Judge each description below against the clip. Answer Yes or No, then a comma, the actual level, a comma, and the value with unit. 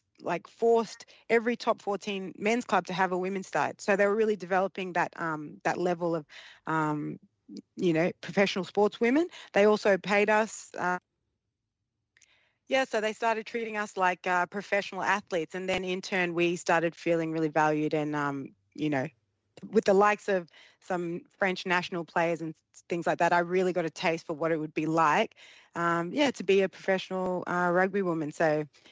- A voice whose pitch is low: No, medium, 185 Hz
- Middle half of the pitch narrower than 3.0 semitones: No, average, 3.3 semitones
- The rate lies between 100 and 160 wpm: No, average, 185 wpm